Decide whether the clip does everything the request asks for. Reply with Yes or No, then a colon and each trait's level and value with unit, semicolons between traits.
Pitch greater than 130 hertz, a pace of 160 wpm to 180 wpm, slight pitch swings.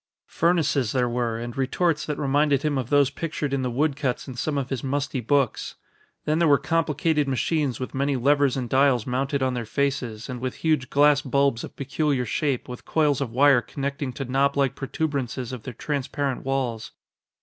No: medium, 140 Hz; average, 190 wpm; narrow, 2.3 semitones